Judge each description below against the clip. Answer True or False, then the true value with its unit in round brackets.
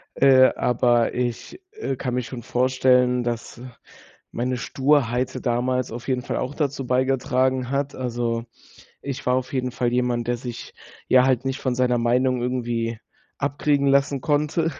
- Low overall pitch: True (125 Hz)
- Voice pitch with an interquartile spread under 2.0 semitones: True (1.6 semitones)